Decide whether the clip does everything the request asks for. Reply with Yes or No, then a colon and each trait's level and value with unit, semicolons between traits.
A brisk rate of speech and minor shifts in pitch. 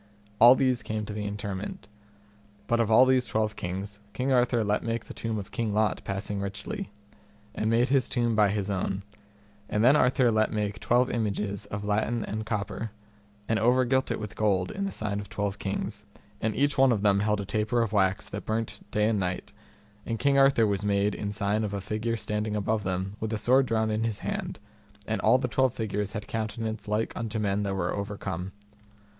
Yes: fast, 210 wpm; narrow, 2.2 semitones